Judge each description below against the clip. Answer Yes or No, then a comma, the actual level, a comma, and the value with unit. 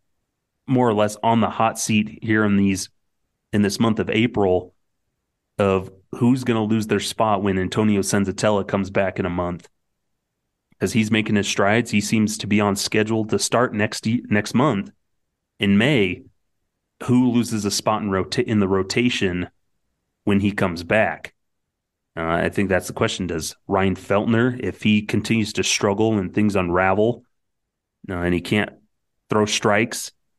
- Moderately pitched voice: No, low, 105 Hz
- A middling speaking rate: Yes, average, 165 wpm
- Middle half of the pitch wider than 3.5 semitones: No, narrow, 2.5 semitones